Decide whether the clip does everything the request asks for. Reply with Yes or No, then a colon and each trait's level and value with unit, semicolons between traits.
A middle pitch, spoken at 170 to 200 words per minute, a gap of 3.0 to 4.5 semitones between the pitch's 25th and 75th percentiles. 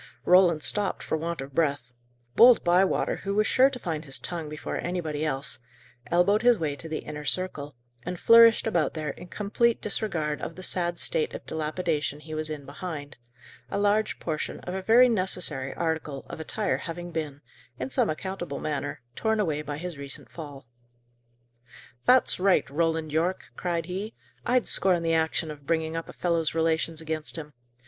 Yes: medium, 165 Hz; average, 175 wpm; average, 3.6 semitones